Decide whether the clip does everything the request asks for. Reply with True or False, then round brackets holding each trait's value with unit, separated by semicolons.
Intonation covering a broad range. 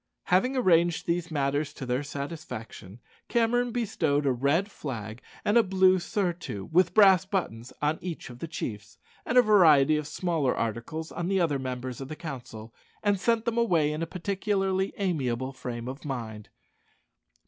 True (6.6 semitones)